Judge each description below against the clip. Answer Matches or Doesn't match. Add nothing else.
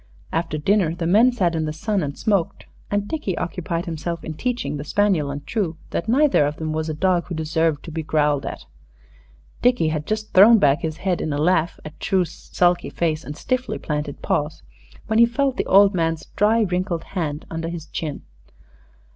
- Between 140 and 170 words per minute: Doesn't match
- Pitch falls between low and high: Matches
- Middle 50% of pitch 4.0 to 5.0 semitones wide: Matches